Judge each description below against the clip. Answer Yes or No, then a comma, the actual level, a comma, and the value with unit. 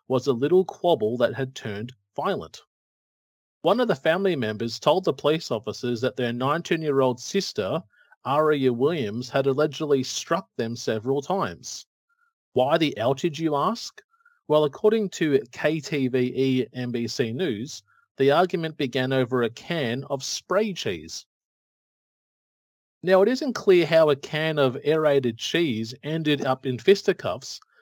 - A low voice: No, medium, 145 Hz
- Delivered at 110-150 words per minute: Yes, average, 140 wpm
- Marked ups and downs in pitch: Yes, wide, 5.7 semitones